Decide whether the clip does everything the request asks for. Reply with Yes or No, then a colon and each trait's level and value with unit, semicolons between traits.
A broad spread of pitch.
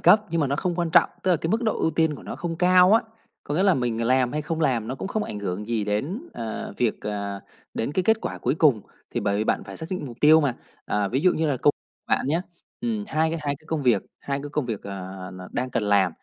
Yes: wide, 7.1 semitones